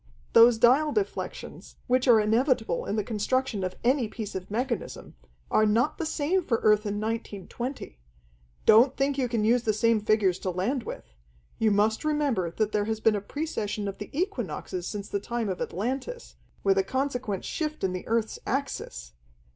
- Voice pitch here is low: No, high, 225 Hz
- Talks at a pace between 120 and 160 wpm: No, average, 180 wpm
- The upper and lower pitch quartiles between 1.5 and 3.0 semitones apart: No, average, 4.1 semitones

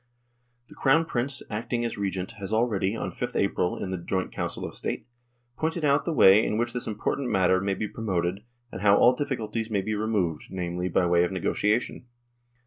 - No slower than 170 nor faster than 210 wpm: Yes, fast, 205 wpm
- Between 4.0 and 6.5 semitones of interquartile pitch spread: Yes, average, 4.3 semitones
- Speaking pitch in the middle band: No, low, 105 Hz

